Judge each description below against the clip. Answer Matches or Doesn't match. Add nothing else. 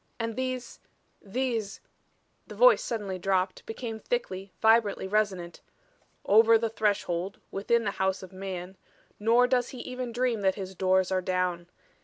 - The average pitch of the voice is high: Matches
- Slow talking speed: Doesn't match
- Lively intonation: Doesn't match